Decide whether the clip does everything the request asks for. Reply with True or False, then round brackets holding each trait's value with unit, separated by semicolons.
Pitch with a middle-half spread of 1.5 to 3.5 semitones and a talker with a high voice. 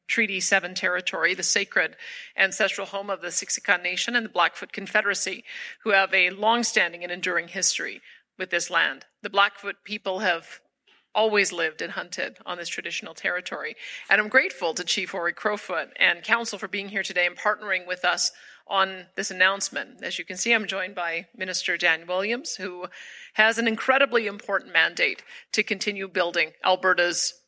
True (2.8 semitones; 195 Hz)